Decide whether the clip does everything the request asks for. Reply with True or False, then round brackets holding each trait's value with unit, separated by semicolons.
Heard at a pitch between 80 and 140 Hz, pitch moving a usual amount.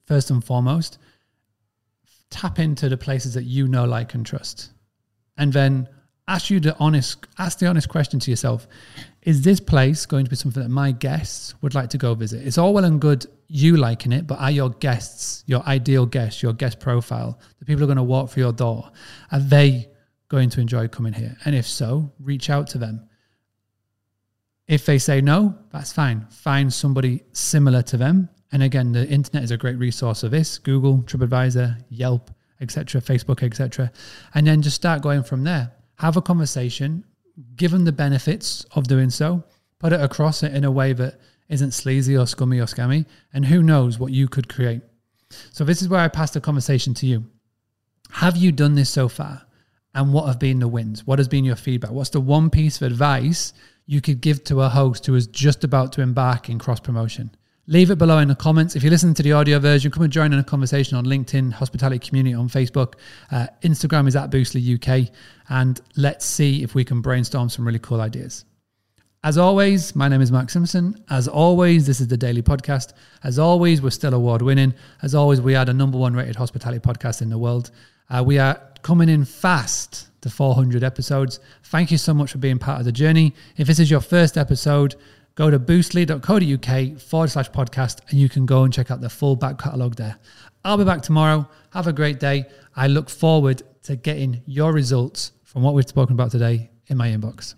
True (135 Hz; 3.2 semitones)